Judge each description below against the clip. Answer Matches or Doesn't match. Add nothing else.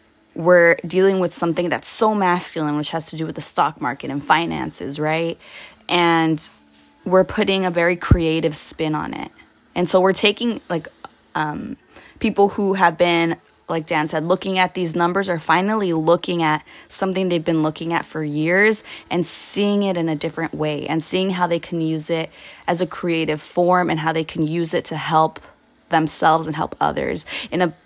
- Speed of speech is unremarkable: Matches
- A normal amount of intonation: Doesn't match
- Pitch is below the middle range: Doesn't match